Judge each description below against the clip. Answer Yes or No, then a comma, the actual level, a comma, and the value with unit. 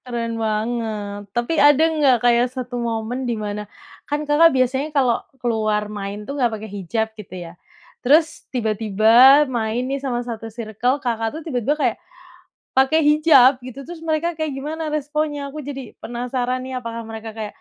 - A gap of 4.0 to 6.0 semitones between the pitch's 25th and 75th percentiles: Yes, average, 4.3 semitones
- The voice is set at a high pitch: Yes, high, 245 Hz